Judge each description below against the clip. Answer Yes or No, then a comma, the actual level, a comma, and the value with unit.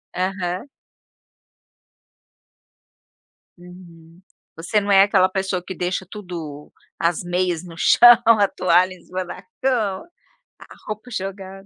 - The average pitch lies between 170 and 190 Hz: Yes, medium, 185 Hz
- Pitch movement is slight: Yes, narrow, 2.0 semitones